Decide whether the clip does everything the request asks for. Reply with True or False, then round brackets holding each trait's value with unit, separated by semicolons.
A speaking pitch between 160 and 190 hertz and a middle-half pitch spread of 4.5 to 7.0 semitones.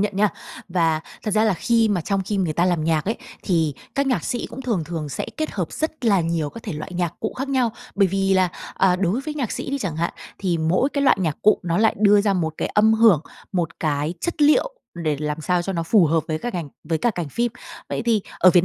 True (185 Hz; 5.2 semitones)